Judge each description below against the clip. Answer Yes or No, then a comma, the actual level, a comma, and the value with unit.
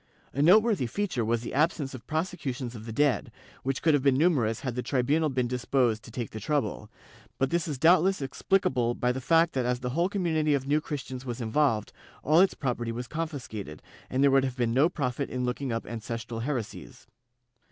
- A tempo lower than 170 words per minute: No, fast, 205 wpm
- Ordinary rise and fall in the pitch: Yes, average, 4.2 semitones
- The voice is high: No, low, 130 Hz